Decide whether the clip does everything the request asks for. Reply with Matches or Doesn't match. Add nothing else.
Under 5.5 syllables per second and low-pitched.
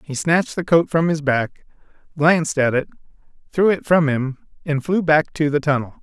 Doesn't match